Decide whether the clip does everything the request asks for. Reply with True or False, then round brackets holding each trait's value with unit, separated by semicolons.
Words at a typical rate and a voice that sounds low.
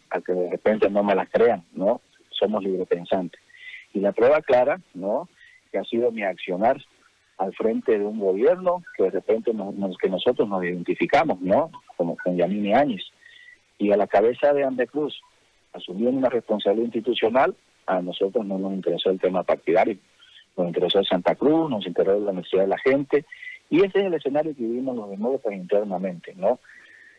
True (180 wpm; 120 Hz)